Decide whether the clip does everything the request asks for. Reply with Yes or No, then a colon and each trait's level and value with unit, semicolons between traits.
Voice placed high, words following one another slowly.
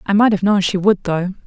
No: high, 195 Hz; fast, 285 wpm